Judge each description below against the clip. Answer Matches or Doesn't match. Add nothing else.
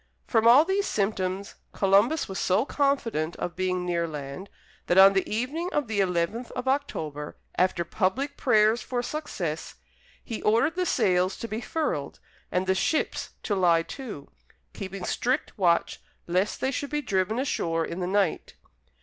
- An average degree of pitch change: Doesn't match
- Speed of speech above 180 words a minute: Doesn't match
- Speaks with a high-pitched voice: Matches